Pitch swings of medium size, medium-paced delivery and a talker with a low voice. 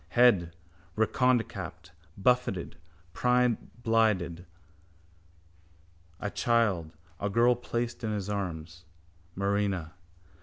No: average, 4.9 semitones; slow, 75 wpm; low, 105 Hz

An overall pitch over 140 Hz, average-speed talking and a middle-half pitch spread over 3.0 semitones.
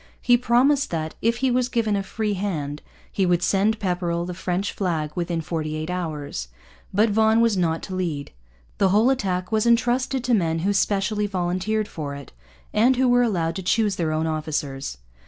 Yes: high, 190 Hz; average, 190 wpm; average, 5.2 semitones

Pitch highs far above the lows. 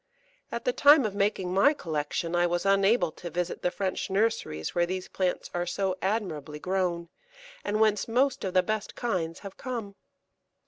No: average, 3.6 semitones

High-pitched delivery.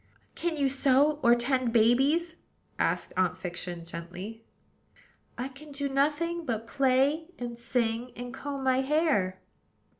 Yes: very high, 260 Hz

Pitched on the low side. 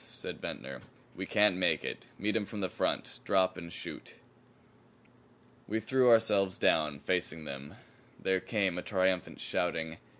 Yes: very low, 95 Hz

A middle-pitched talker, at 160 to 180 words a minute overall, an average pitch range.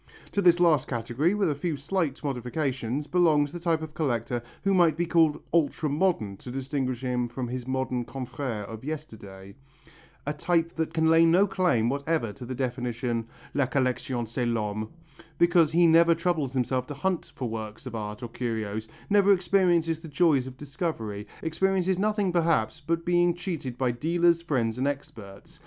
No: medium, 145 Hz; average, 175 wpm; wide, 5.7 semitones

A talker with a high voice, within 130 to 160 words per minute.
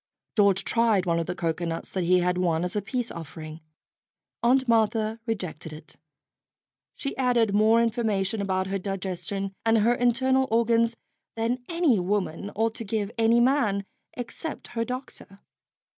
Yes: high, 215 Hz; average, 155 wpm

